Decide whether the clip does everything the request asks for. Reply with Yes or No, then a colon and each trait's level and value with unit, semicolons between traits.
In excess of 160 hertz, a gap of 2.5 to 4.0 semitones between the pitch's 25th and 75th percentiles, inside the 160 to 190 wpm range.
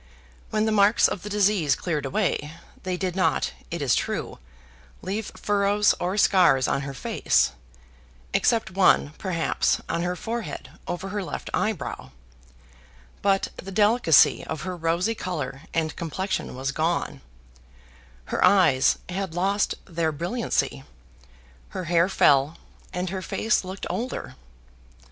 No: medium, 185 Hz; average, 3.7 semitones; slow, 135 wpm